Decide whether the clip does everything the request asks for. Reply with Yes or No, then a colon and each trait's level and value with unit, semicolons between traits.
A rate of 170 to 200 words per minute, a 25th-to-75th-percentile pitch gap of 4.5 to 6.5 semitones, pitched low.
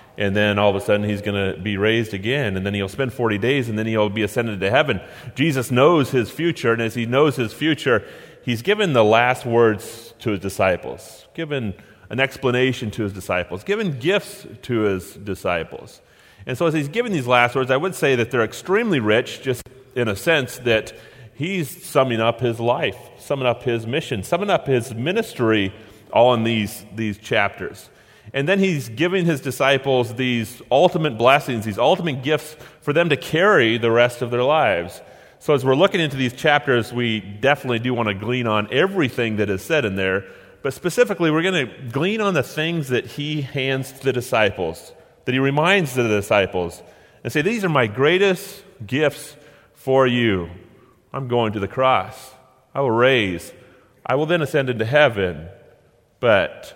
Yes: average, 185 wpm; average, 5.1 semitones; low, 125 Hz